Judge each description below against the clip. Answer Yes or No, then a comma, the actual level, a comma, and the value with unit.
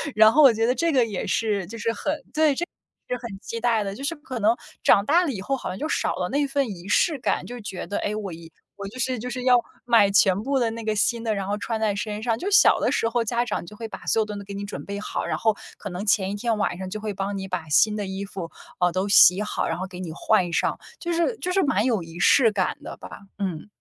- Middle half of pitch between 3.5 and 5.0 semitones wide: Yes, average, 3.8 semitones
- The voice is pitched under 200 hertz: No, high, 215 Hz